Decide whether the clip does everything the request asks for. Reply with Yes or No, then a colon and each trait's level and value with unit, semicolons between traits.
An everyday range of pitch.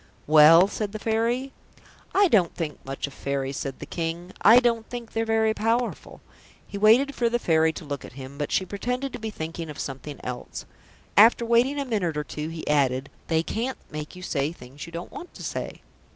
No: wide, 7.4 semitones